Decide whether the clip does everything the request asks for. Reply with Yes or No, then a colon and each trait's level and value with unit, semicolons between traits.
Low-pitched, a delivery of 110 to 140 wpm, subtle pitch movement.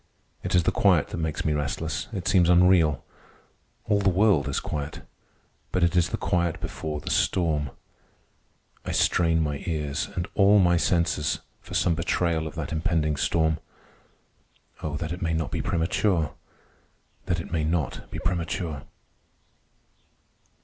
No: very low, 80 Hz; average, 150 wpm; narrow, 2.2 semitones